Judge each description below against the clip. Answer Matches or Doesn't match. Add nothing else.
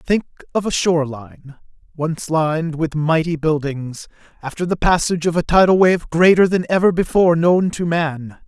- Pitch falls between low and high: Matches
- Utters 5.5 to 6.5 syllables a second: Doesn't match